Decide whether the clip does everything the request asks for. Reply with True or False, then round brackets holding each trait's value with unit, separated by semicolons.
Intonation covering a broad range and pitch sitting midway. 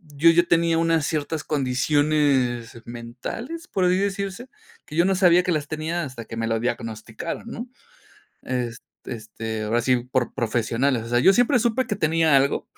True (6.3 semitones; 145 Hz)